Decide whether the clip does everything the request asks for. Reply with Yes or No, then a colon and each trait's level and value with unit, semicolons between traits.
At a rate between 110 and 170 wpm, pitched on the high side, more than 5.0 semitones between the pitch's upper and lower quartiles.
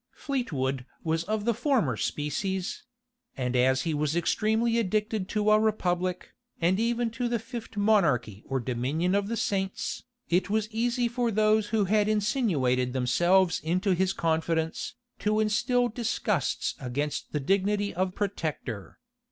Yes: average, 145 wpm; high, 195 Hz; wide, 5.5 semitones